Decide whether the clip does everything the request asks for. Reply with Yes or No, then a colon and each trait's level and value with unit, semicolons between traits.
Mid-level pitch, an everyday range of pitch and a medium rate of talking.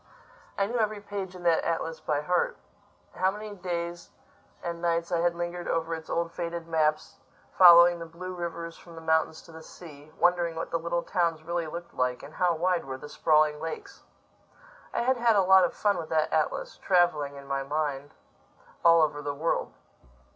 No: medium, 170 Hz; narrow, 2.0 semitones; average, 190 wpm